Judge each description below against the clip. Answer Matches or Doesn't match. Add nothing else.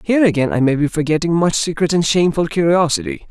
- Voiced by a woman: Doesn't match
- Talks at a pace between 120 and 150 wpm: Doesn't match